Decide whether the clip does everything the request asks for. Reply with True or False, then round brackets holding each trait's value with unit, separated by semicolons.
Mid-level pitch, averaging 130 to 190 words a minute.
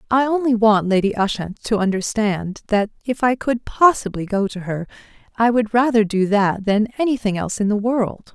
False (220 Hz; 185 wpm)